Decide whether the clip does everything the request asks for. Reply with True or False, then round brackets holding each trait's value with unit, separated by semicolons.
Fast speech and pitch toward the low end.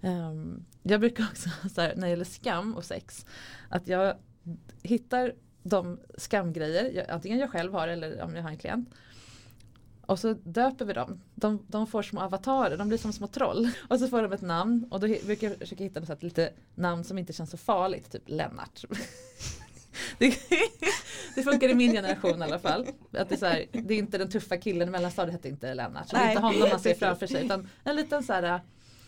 False (215 wpm; 195 Hz)